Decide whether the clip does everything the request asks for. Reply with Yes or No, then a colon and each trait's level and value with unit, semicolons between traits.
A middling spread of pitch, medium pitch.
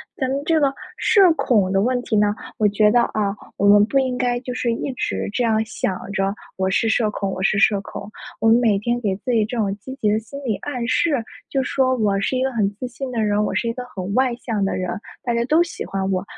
No: average, 3.8 semitones; high, 225 Hz